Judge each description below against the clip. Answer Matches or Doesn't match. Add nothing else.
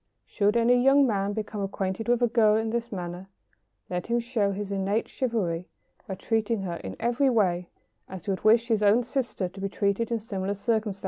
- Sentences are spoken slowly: Doesn't match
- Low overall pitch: Doesn't match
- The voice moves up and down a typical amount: Matches